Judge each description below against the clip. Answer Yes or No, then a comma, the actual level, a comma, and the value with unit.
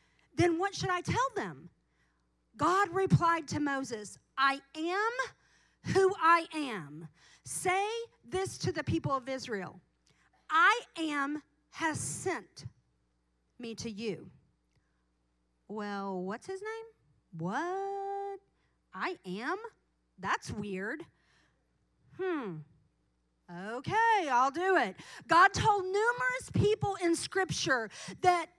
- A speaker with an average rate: No, slow, 105 wpm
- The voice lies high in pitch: Yes, very high, 320 Hz